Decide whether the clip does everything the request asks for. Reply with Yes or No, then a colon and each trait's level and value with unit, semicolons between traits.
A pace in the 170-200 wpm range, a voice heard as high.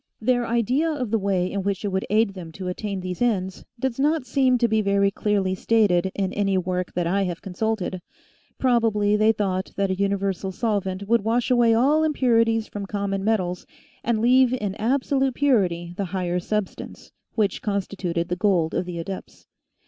Yes: average, 180 wpm; high, 200 Hz